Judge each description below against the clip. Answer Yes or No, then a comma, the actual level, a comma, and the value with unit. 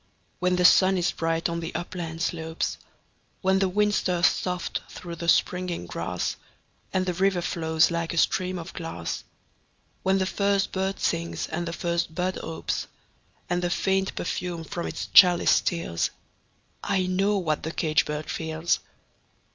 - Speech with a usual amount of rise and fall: No, narrow, 2.2 semitones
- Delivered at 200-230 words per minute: No, average, 160 wpm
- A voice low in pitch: No, medium, 175 Hz